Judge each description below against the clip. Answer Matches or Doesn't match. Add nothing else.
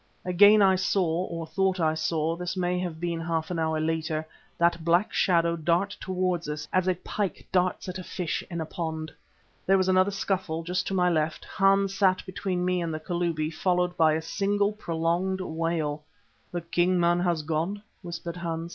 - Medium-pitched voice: Matches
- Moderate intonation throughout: Doesn't match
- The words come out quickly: Doesn't match